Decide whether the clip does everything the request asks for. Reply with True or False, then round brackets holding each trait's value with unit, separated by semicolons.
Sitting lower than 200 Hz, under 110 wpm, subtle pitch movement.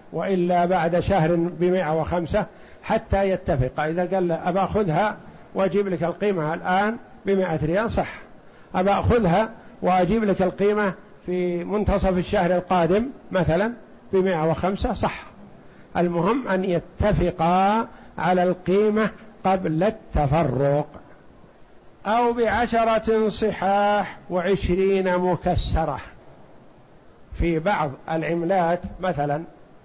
False (185 Hz; 95 wpm; 3.0 semitones)